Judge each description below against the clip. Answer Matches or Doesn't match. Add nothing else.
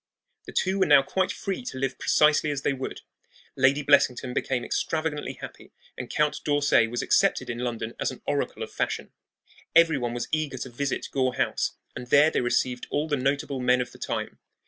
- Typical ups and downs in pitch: Matches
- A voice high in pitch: Doesn't match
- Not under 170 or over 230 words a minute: Matches